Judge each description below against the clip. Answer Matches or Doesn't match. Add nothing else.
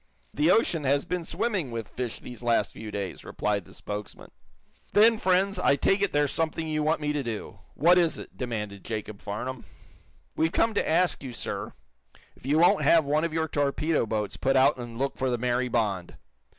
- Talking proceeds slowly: Doesn't match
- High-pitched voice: Doesn't match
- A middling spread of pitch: Doesn't match